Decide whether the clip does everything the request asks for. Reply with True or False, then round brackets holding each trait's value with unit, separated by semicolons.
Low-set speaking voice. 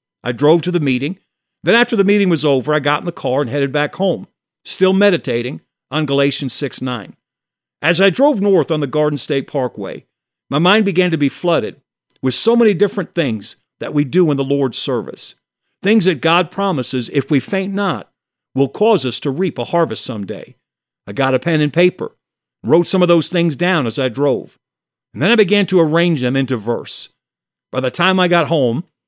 False (160 Hz)